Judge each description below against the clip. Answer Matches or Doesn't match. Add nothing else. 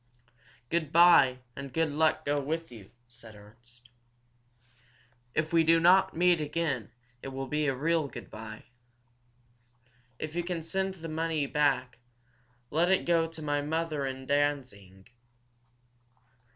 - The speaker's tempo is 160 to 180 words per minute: Doesn't match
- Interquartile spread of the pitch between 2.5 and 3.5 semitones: Doesn't match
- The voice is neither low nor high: Matches